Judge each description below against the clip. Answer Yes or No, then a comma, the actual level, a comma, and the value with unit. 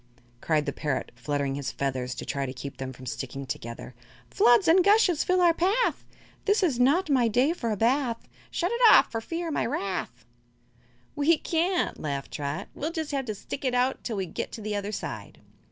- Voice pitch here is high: Yes, high, 235 Hz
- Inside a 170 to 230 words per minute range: Yes, average, 200 wpm